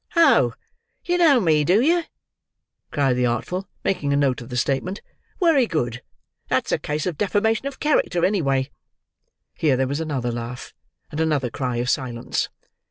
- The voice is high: No, medium, 150 Hz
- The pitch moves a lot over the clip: Yes, wide, 8.2 semitones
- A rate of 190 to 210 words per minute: No, average, 165 wpm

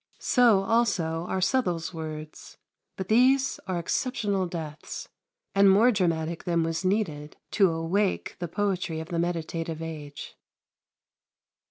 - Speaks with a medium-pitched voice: Yes, medium, 175 Hz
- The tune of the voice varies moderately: Yes, average, 3.7 semitones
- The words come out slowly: Yes, slow, 125 wpm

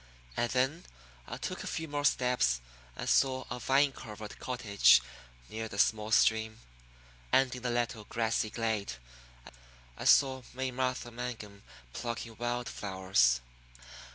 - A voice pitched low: Yes, low, 120 Hz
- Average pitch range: Yes, average, 3.0 semitones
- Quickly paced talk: No, slow, 135 wpm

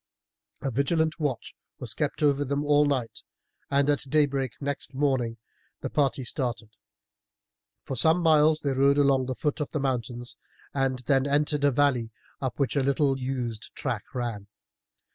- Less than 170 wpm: Yes, average, 160 wpm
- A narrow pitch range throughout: Yes, narrow, 2.3 semitones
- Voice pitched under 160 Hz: Yes, medium, 140 Hz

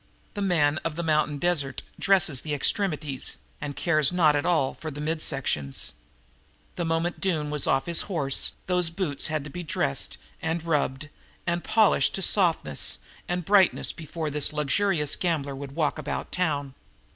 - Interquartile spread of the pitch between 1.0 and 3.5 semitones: Yes, average, 3.2 semitones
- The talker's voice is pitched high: No, medium, 155 Hz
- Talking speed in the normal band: Yes, average, 165 wpm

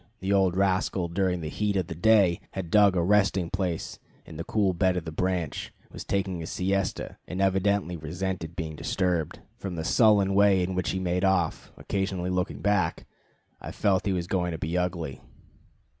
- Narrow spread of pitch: Yes, narrow, 2.2 semitones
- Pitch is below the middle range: Yes, very low, 90 Hz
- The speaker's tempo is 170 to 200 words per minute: Yes, average, 190 wpm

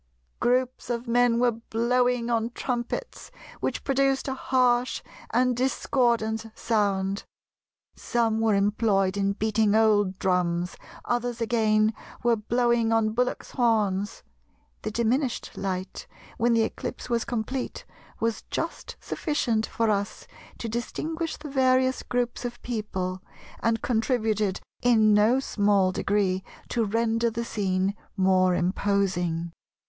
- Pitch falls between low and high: No, high, 225 Hz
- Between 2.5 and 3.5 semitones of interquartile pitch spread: Yes, average, 3.1 semitones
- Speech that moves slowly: Yes, slow, 120 wpm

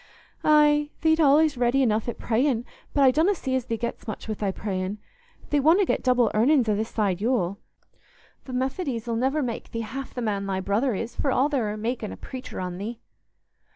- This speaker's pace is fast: Yes, fast, 210 wpm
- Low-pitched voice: No, high, 240 Hz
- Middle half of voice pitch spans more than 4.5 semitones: No, average, 4.2 semitones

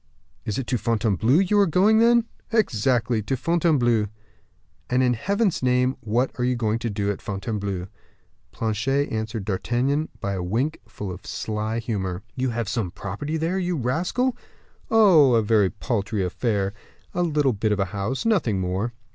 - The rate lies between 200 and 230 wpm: No, average, 165 wpm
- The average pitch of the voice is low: Yes, low, 120 Hz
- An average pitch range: No, wide, 5.9 semitones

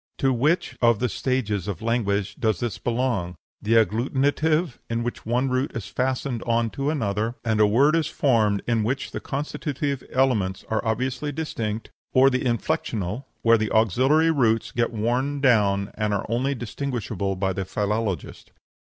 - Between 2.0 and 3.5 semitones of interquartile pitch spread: No, average, 3.9 semitones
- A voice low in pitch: Yes, low, 115 Hz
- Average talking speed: Yes, average, 165 wpm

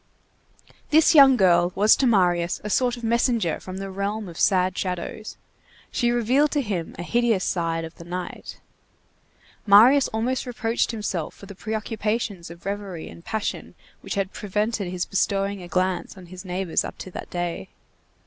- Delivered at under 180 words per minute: Yes, average, 170 wpm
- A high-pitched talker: Yes, high, 200 Hz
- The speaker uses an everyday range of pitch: Yes, average, 4.1 semitones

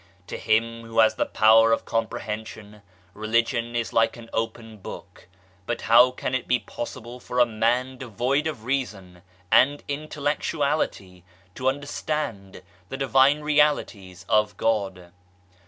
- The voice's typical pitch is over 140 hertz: No, low, 115 Hz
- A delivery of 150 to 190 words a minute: No, average, 140 wpm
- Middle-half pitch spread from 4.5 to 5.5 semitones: No, average, 3.5 semitones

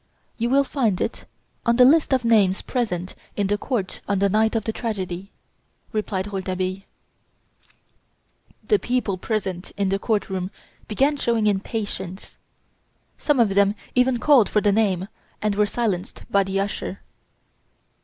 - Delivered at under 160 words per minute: Yes, average, 150 wpm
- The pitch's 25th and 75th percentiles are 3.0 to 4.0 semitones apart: Yes, average, 3.5 semitones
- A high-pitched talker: Yes, high, 205 Hz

